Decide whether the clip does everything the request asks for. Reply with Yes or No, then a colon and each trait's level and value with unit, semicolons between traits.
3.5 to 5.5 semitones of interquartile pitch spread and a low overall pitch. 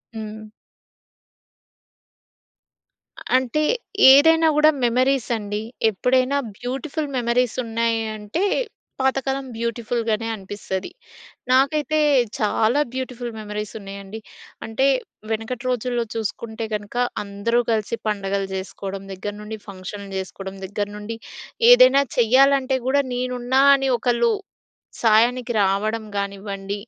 No: average, 3.8 semitones; high, 230 Hz